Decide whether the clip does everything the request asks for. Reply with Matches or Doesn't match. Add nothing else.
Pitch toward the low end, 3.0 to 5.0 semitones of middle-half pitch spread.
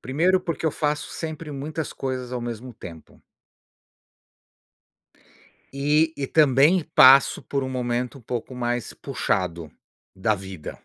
Matches